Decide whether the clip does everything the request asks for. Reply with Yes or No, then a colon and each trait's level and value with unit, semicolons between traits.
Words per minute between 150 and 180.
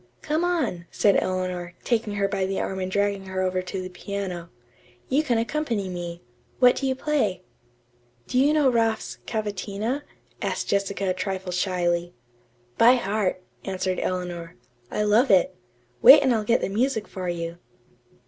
Yes: average, 160 wpm